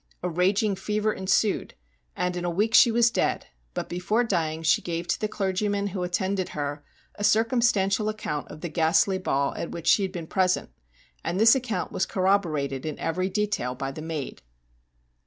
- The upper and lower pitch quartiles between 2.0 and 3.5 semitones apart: No, average, 4.1 semitones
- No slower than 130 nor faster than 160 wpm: No, average, 185 wpm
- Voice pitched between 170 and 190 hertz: Yes, medium, 185 Hz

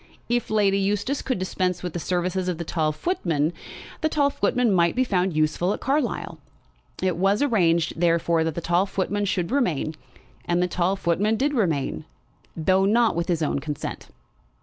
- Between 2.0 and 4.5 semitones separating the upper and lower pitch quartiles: Yes, average, 3.9 semitones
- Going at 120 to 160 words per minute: No, average, 175 wpm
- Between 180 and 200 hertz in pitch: Yes, medium, 185 Hz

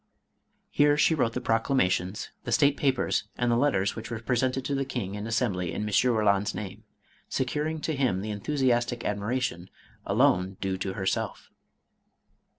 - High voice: No, low, 115 Hz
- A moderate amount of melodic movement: Yes, average, 4.8 semitones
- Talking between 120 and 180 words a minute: Yes, average, 160 wpm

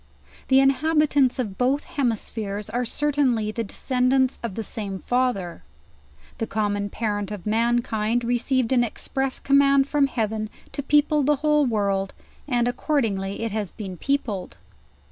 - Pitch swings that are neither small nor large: Yes, average, 4.3 semitones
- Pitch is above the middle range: Yes, high, 240 Hz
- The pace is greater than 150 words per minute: No, average, 145 wpm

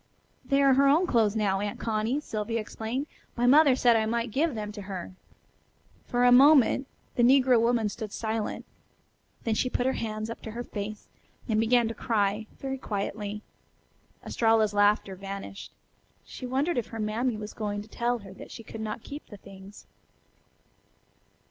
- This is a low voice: No, high, 225 Hz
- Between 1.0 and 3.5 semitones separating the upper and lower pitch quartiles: Yes, average, 2.9 semitones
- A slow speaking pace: No, average, 175 wpm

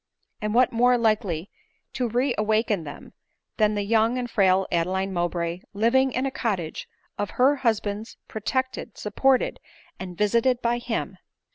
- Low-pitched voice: No, high, 220 Hz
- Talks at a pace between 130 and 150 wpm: Yes, average, 145 wpm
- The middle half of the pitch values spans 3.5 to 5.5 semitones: Yes, average, 4.2 semitones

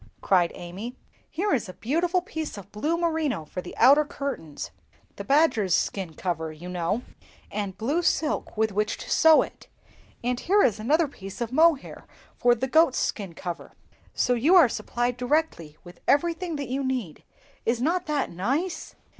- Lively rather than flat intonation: Yes, wide, 8.3 semitones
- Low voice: No, very high, 250 Hz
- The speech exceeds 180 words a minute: No, average, 170 wpm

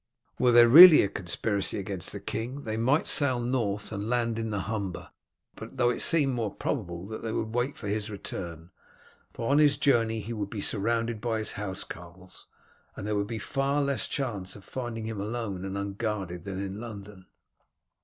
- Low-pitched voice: Yes, low, 110 Hz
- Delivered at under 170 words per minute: No, average, 185 wpm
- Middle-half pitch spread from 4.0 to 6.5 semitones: No, average, 3.3 semitones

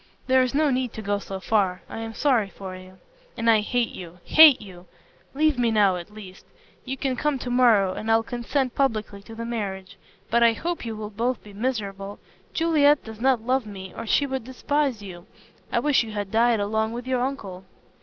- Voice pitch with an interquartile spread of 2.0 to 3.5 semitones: No, average, 4.3 semitones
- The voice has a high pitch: Yes, high, 225 Hz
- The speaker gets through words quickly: Yes, fast, 210 wpm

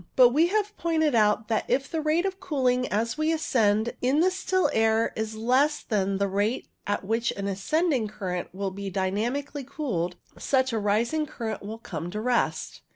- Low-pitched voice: No, high, 230 Hz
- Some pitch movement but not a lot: No, wide, 6.5 semitones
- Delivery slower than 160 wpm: No, average, 185 wpm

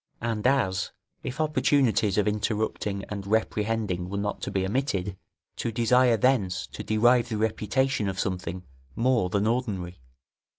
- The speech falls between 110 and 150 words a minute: Yes, average, 140 wpm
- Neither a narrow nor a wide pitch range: Yes, average, 3.7 semitones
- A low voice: Yes, low, 110 Hz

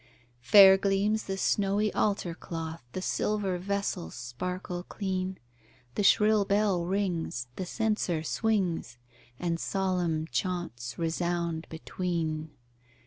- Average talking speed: No, slow, 105 wpm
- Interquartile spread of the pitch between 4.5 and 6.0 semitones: No, average, 3.2 semitones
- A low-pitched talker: No, medium, 180 Hz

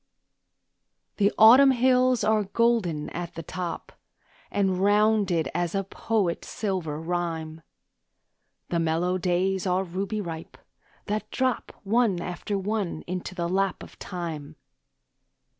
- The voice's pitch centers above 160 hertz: Yes, medium, 185 Hz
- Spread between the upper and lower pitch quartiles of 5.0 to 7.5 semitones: No, average, 3.6 semitones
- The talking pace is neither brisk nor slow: No, slow, 120 wpm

